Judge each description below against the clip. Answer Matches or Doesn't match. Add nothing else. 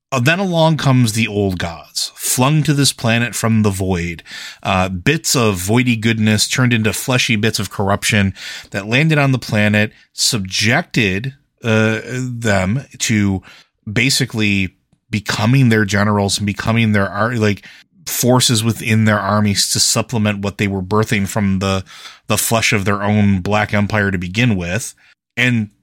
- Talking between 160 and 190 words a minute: Doesn't match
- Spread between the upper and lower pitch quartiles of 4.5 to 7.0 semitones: Doesn't match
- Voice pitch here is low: Matches